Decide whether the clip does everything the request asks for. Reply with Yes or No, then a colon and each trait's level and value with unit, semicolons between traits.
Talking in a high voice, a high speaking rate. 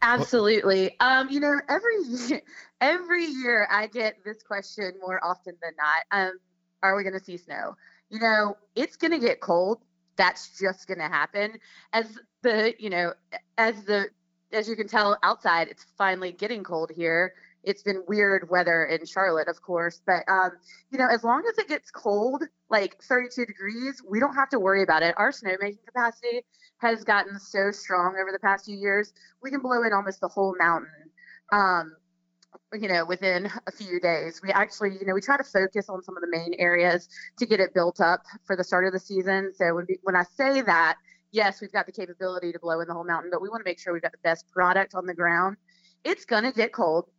Yes: high, 195 Hz; fast, 210 wpm